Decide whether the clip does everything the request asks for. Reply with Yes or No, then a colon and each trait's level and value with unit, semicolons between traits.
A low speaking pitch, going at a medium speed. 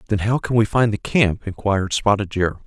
No: low, 105 Hz; fast, 225 wpm